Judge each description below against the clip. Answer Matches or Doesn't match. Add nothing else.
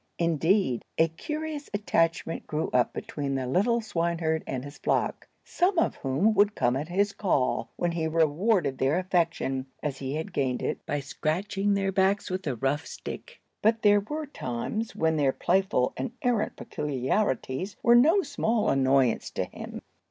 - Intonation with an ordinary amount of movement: Doesn't match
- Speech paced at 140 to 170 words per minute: Matches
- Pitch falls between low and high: Matches